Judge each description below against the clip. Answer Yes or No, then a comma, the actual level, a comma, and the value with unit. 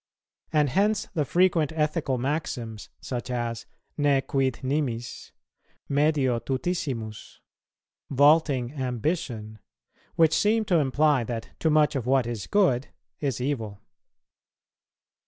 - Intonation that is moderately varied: Yes, average, 4.3 semitones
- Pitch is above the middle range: No, low, 135 Hz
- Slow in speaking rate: Yes, slow, 110 wpm